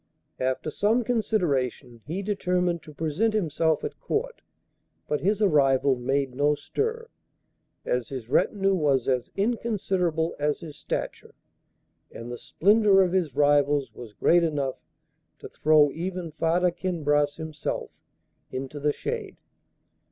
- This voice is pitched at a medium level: Yes, medium, 160 Hz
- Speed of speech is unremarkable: No, slow, 130 wpm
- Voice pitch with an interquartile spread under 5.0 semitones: No, average, 5.3 semitones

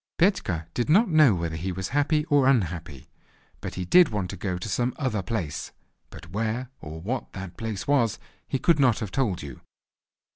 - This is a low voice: Yes, low, 110 Hz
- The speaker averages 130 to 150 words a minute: No, average, 190 wpm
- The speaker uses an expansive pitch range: Yes, wide, 7.3 semitones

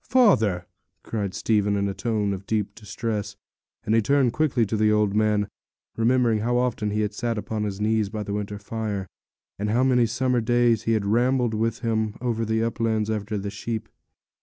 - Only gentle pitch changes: Yes, narrow, 2.0 semitones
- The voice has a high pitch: No, low, 110 Hz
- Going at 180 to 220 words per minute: Yes, average, 190 wpm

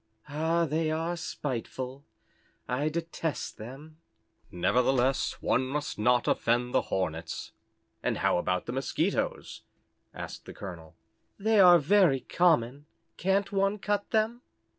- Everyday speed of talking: No, slow, 120 wpm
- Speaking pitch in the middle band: Yes, medium, 145 Hz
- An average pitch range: No, wide, 5.8 semitones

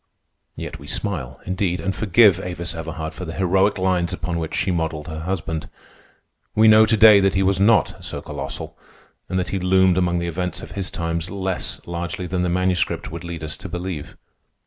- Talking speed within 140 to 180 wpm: No, average, 195 wpm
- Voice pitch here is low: Yes, very low, 90 Hz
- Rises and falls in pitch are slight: Yes, narrow, 2.1 semitones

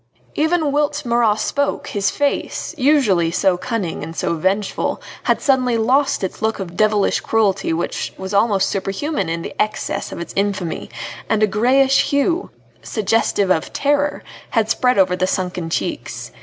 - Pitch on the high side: Yes, high, 215 Hz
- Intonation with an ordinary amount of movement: No, wide, 6.1 semitones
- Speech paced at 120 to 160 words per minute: Yes, average, 155 wpm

